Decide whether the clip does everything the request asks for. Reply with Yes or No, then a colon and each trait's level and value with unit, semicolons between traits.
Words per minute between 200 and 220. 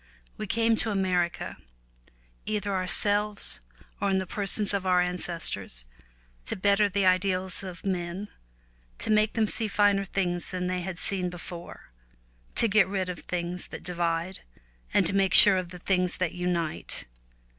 No: average, 155 wpm